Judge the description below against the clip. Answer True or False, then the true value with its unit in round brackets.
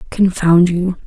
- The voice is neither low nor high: True (180 Hz)